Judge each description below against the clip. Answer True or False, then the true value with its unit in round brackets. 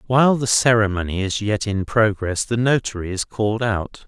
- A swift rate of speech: False (175 wpm)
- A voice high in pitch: False (110 Hz)